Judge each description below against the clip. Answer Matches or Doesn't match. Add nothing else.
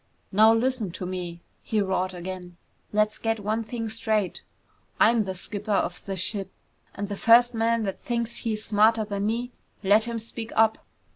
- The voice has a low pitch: Doesn't match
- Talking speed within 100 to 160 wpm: Doesn't match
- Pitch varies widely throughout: Doesn't match